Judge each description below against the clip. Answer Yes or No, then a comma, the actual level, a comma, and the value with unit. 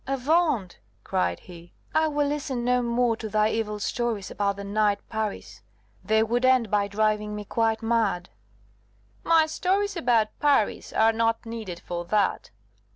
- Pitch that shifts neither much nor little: Yes, average, 3.2 semitones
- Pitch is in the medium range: No, high, 225 Hz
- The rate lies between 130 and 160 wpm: Yes, average, 155 wpm